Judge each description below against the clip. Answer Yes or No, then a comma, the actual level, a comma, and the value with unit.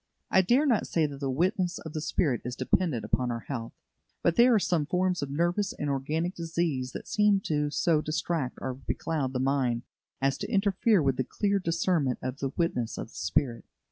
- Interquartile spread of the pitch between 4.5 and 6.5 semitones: Yes, wide, 5.4 semitones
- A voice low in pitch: No, medium, 155 Hz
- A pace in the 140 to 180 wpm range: No, fast, 205 wpm